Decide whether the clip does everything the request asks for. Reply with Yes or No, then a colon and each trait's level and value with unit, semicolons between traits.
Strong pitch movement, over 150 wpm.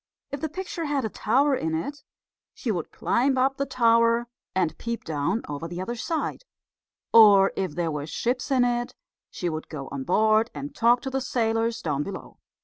Yes: wide, 7.0 semitones; average, 190 wpm